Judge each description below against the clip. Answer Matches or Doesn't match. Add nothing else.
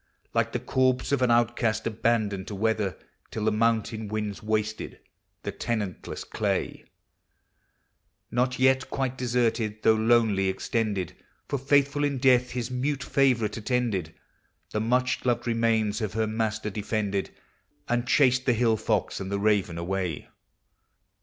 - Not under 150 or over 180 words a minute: Doesn't match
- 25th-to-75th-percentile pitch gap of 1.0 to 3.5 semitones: Matches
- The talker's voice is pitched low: Matches